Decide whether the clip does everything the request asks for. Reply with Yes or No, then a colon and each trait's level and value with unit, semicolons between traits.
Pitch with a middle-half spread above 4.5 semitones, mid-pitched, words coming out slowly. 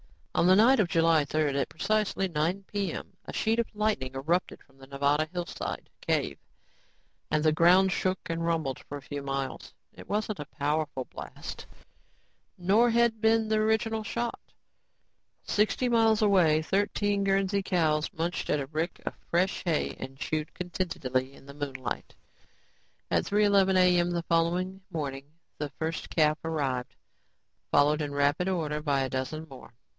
No: average, 5.3 semitones; medium, 165 Hz; average, 155 wpm